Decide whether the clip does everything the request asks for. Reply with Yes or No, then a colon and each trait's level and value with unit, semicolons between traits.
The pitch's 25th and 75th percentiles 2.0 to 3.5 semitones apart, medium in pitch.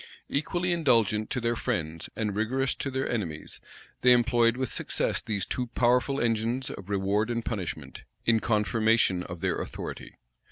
No: average, 3.1 semitones; low, 115 Hz